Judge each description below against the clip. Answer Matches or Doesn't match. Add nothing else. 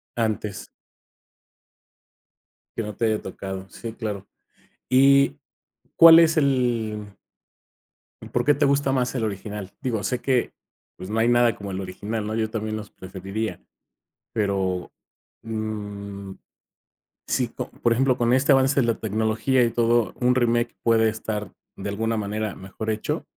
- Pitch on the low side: Matches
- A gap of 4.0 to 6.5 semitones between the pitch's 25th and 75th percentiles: Doesn't match